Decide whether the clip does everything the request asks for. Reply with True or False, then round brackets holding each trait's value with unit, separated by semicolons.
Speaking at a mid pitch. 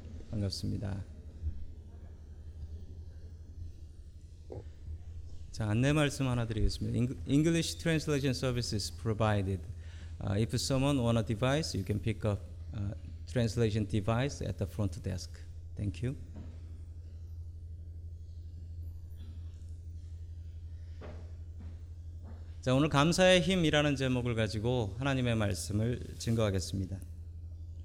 False (85 Hz)